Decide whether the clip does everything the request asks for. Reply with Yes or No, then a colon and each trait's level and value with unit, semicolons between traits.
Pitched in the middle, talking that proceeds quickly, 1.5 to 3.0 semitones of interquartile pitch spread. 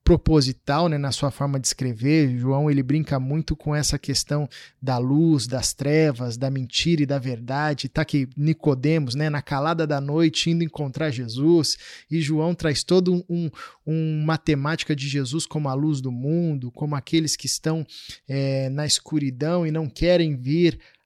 No: medium, 150 Hz; average, 170 wpm; narrow, 2.6 semitones